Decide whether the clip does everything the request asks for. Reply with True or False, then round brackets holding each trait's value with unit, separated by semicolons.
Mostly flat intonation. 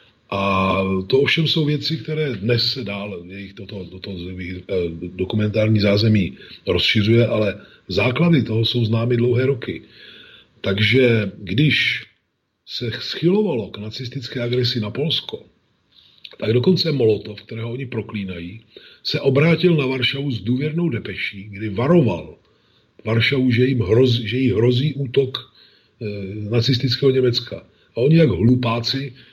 False (4.1 semitones)